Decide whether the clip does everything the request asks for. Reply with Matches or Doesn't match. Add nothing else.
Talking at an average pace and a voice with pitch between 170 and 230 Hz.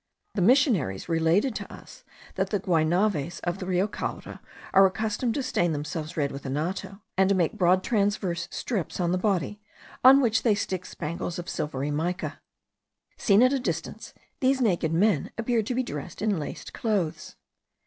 Matches